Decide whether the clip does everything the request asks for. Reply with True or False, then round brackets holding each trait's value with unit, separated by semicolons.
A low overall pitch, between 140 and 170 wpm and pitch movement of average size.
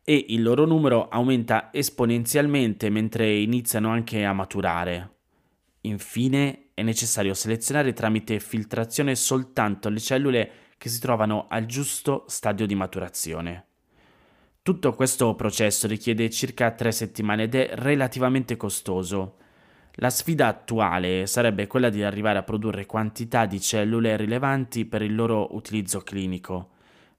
False (110 Hz; 125 wpm; 3.1 semitones)